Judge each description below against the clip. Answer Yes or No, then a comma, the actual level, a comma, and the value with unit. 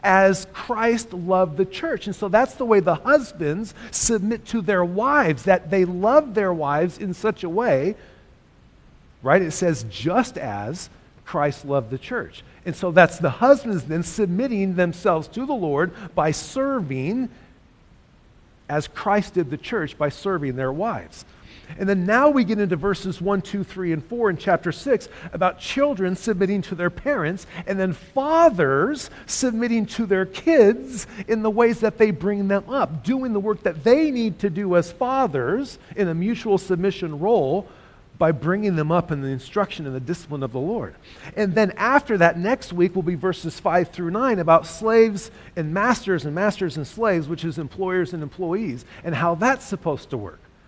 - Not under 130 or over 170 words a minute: No, average, 180 wpm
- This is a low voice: No, high, 190 Hz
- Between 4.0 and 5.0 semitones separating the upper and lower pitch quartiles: Yes, average, 4.7 semitones